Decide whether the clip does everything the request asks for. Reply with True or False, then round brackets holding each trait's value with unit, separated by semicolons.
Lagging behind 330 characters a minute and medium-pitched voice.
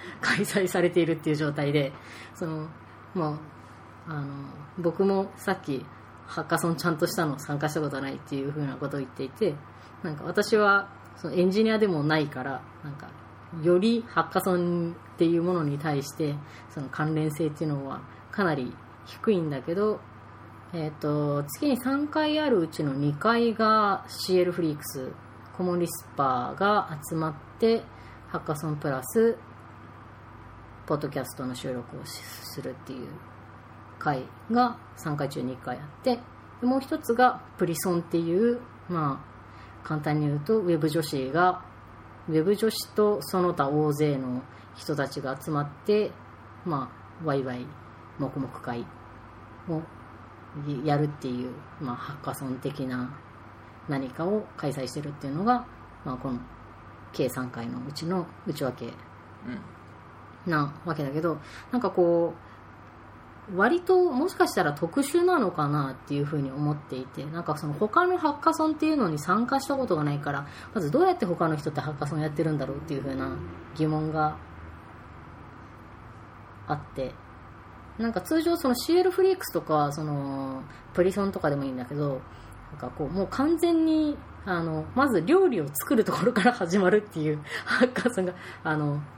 True (305 characters per minute; 150 Hz)